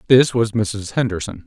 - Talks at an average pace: Yes, average, 165 wpm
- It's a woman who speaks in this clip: No, male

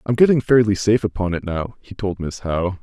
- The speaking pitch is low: Yes, low, 100 Hz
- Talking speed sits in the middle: No, fast, 235 wpm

